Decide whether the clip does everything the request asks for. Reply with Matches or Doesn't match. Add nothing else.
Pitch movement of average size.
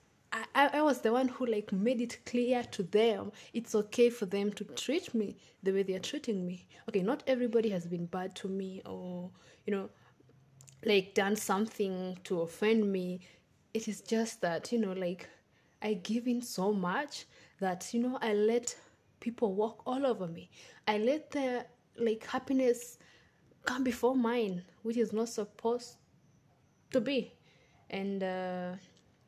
Matches